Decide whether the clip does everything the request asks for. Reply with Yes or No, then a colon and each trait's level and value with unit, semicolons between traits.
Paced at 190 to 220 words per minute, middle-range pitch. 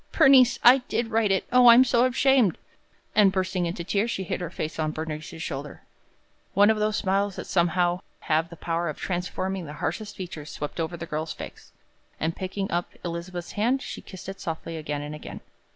Yes: average, 200 wpm; medium, 180 Hz